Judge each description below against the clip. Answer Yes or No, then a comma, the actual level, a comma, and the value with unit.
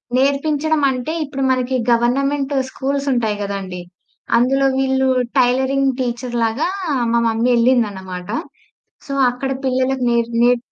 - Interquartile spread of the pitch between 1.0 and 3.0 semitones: Yes, narrow, 2.5 semitones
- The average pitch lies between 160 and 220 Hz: No, very high, 255 Hz